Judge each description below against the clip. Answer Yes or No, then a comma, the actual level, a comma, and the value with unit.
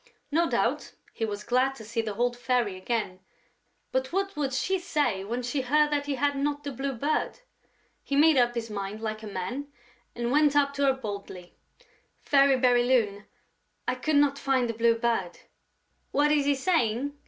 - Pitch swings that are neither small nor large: Yes, average, 4.0 semitones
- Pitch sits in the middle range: No, very high, 255 Hz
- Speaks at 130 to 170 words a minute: No, average, 185 wpm